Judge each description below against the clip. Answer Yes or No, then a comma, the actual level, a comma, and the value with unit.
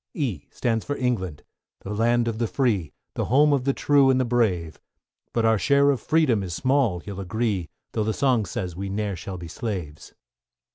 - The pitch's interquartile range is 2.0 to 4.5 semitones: No, wide, 5.5 semitones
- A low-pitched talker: Yes, low, 110 Hz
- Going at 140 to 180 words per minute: No, average, 195 wpm